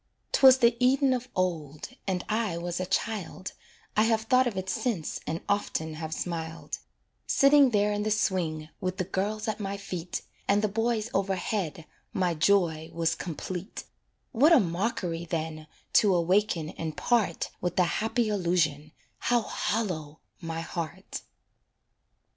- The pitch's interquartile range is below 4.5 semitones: No, average, 4.8 semitones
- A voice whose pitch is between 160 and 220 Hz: Yes, high, 190 Hz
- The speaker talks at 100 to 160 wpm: Yes, average, 150 wpm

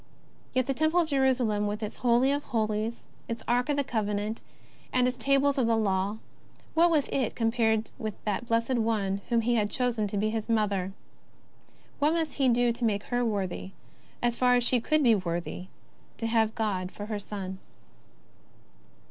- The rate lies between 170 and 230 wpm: Yes, average, 180 wpm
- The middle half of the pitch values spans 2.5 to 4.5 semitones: Yes, average, 3.2 semitones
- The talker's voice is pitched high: Yes, high, 230 Hz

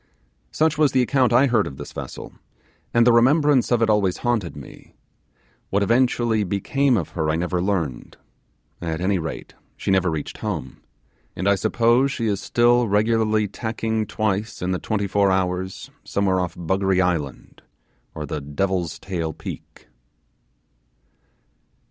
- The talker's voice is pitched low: Yes, low, 100 Hz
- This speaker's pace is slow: No, average, 150 wpm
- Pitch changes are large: No, average, 4.6 semitones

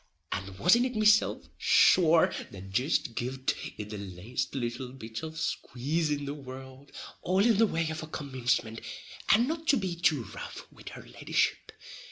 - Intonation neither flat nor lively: No, wide, 6.6 semitones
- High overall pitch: No, medium, 140 Hz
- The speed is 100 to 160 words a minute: No, average, 175 wpm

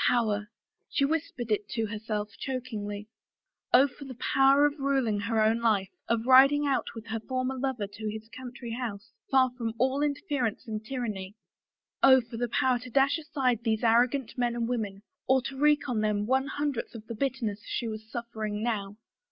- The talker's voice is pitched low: No, high, 240 Hz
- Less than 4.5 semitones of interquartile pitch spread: Yes, average, 3.5 semitones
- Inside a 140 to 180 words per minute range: No, average, 190 wpm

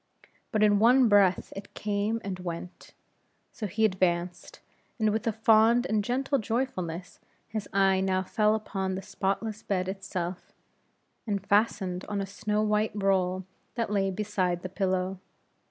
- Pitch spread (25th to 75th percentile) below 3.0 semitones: Yes, narrow, 2.5 semitones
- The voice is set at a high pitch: Yes, high, 200 Hz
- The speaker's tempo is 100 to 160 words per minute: Yes, average, 150 wpm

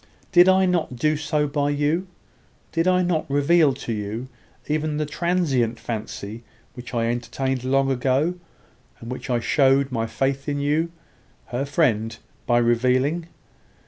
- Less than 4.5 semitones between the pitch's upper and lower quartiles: Yes, average, 4.1 semitones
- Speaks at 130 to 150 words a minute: Yes, average, 145 wpm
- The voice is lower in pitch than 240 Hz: Yes, medium, 140 Hz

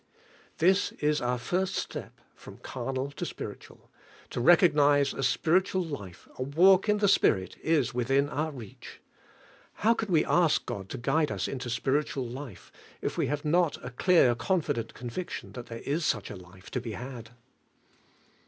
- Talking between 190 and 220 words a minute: No, average, 170 wpm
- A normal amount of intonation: No, wide, 5.8 semitones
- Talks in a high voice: No, medium, 140 Hz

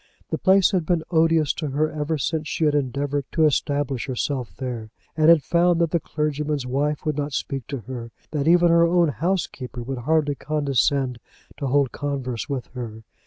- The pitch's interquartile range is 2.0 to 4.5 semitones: Yes, average, 3.1 semitones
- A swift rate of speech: No, average, 185 wpm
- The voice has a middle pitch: Yes, medium, 145 Hz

